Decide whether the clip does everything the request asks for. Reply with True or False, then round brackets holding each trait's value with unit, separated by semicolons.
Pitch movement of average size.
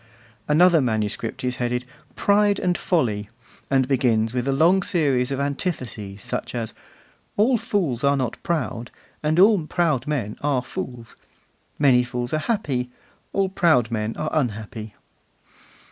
False (5.7 semitones)